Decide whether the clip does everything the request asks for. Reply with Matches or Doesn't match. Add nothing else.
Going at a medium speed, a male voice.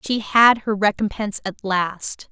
Doesn't match